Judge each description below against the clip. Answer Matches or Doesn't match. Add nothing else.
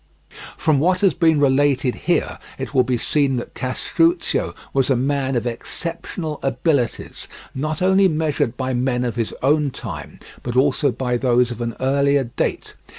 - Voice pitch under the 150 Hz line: Matches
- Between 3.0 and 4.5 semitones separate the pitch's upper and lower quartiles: Matches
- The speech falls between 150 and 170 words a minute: Matches